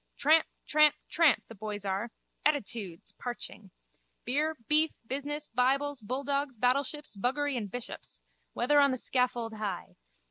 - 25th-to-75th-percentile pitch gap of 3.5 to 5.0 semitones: Yes, average, 4.5 semitones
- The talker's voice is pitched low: No, very high, 255 Hz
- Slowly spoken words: Yes, slow, 130 wpm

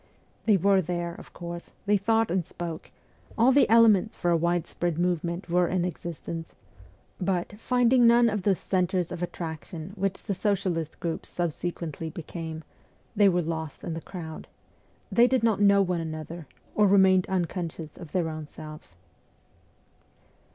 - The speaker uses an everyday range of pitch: Yes, average, 3.2 semitones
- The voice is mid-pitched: Yes, medium, 175 Hz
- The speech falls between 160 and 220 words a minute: No, average, 150 wpm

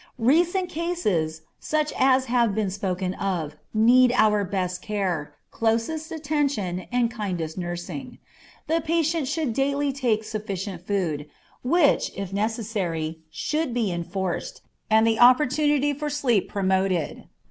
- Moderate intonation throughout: No, wide, 7.1 semitones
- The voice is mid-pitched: No, high, 220 Hz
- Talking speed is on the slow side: Yes, slow, 125 wpm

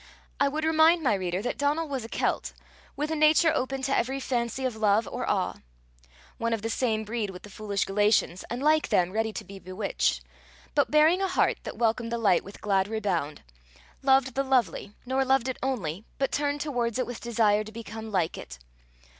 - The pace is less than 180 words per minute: No, fast, 205 wpm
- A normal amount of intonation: Yes, average, 4.7 semitones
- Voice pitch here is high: Yes, high, 235 Hz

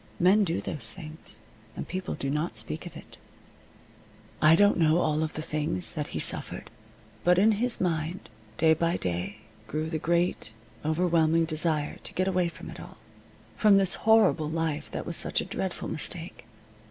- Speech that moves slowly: No, average, 170 wpm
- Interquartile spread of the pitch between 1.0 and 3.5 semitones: Yes, average, 2.9 semitones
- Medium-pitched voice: Yes, medium, 165 Hz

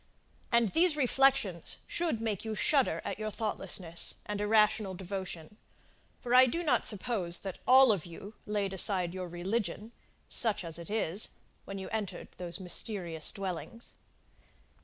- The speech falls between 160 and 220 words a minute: No, average, 145 wpm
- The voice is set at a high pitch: Yes, high, 205 Hz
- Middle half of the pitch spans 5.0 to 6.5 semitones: No, average, 4.2 semitones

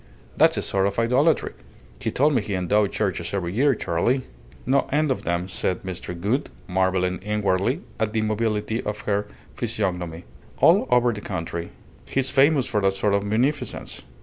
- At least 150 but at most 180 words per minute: Yes, average, 170 wpm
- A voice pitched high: No, low, 105 Hz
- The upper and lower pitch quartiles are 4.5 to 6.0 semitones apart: Yes, average, 4.8 semitones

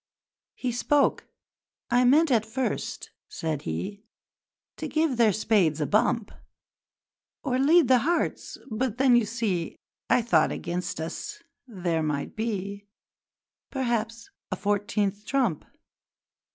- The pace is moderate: No, slow, 120 wpm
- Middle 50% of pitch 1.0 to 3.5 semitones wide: No, average, 4.8 semitones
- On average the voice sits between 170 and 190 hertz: No, high, 225 Hz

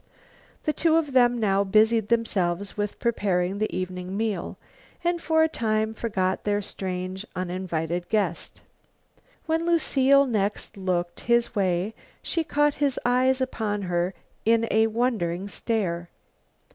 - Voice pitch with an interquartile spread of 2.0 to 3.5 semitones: No, average, 4.8 semitones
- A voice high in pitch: Yes, high, 215 Hz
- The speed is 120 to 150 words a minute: Yes, slow, 135 wpm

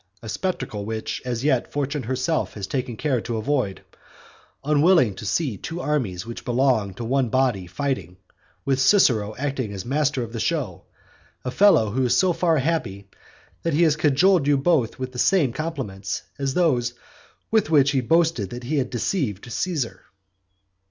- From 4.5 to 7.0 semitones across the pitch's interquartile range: Yes, average, 5.1 semitones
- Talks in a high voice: No, low, 130 Hz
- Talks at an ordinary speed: Yes, average, 170 wpm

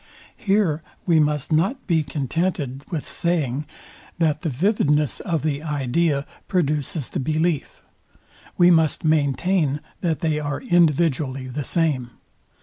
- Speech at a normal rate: No, slow, 125 wpm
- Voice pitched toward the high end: No, medium, 155 Hz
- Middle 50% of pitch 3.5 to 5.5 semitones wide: No, average, 3.0 semitones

